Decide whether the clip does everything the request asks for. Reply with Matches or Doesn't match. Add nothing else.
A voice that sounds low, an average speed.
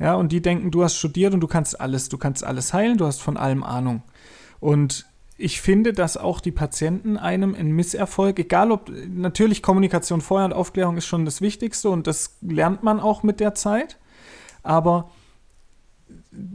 Doesn't match